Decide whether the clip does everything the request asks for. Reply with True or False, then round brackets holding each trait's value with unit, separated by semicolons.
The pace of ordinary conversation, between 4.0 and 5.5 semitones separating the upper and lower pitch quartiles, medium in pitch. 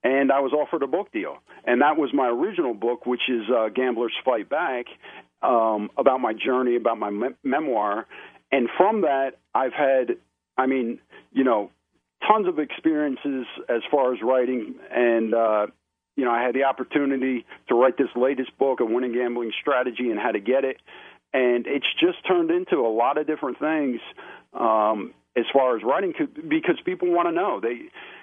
False (185 wpm; 4.4 semitones; 130 Hz)